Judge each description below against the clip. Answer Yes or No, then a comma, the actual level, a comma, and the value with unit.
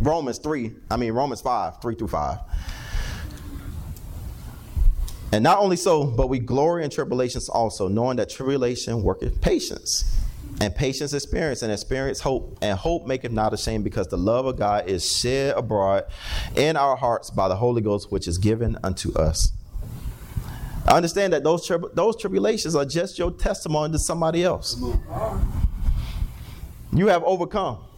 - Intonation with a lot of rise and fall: Yes, wide, 8.0 semitones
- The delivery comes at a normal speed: Yes, average, 155 wpm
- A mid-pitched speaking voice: No, low, 120 Hz